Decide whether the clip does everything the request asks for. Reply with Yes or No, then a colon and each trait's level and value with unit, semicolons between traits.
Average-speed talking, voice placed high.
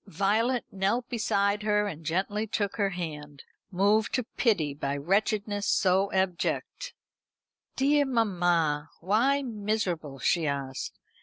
No: slow, 120 wpm; high, 200 Hz